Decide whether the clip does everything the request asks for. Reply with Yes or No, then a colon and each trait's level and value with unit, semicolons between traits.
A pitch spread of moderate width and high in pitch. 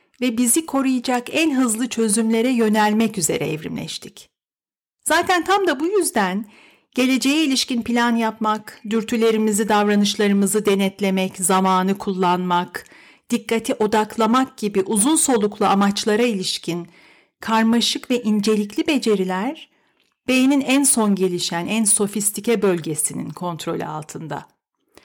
Yes: average, 4.2 semitones; high, 220 Hz